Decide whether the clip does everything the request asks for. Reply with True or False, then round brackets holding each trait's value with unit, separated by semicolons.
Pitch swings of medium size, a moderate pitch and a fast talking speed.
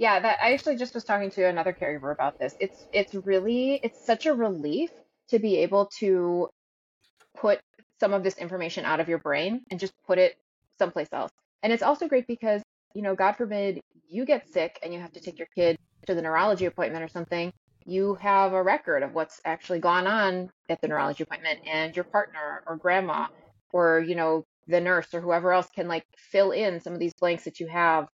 True (3.4 semitones; 180 Hz; 215 wpm)